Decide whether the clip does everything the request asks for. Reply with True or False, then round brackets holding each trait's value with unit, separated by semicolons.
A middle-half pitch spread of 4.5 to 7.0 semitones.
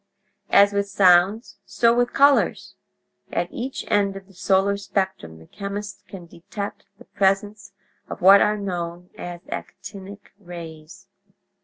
False (2.4 semitones)